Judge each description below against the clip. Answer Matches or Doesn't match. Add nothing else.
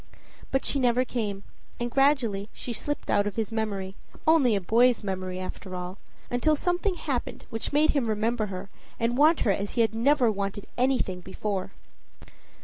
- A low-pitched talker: Doesn't match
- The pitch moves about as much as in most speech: Matches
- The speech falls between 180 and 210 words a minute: Doesn't match